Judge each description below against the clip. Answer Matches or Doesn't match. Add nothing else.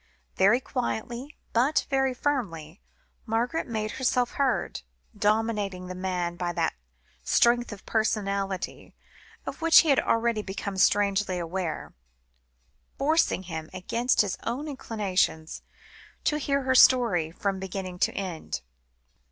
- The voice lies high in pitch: Matches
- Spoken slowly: Matches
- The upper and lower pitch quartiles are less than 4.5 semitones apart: Doesn't match